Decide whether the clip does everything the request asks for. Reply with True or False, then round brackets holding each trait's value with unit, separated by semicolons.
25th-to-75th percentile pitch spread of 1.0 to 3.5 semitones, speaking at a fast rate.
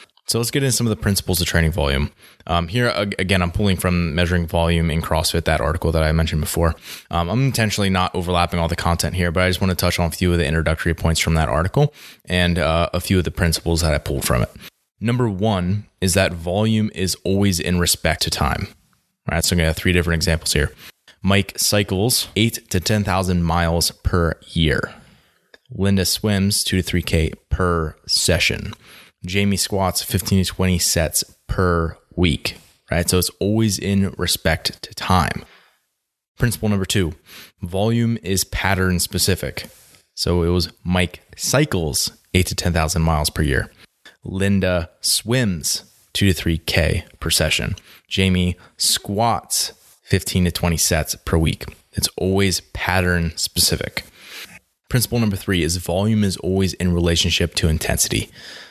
False (2.7 semitones; 170 wpm)